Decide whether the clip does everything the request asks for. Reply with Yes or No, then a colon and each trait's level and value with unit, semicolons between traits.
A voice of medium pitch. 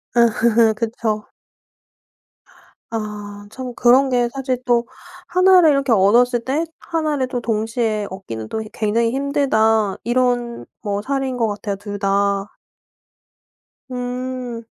No: high, 235 Hz